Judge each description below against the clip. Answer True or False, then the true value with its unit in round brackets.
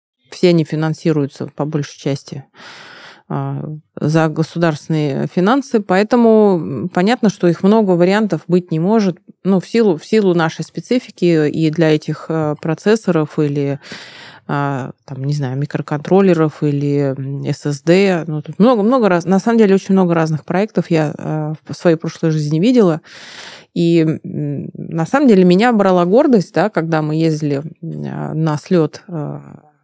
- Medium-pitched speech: True (165 Hz)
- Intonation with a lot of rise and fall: False (3.7 semitones)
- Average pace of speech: True (135 wpm)